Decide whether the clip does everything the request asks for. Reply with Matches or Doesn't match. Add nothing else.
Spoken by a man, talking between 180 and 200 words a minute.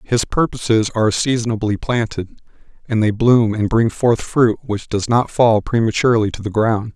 Doesn't match